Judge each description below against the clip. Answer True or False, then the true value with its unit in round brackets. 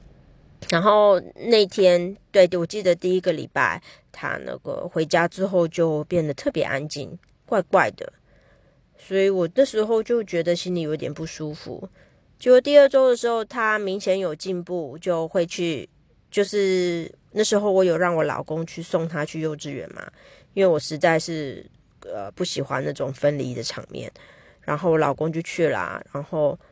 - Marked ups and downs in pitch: False (3.8 semitones)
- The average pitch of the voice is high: False (175 Hz)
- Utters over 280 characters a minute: False (245 characters per minute)